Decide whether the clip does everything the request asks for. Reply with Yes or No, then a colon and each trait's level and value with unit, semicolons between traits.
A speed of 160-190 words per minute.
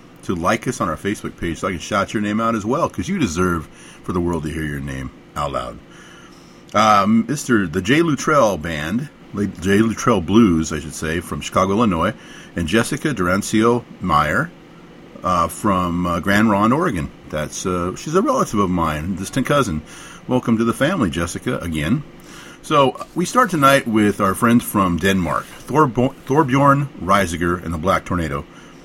Yes: average, 175 wpm